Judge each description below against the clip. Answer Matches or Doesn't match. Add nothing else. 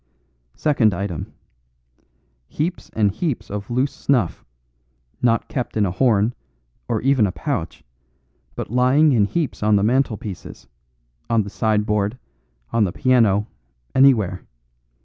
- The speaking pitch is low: Matches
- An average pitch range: Matches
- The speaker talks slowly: Matches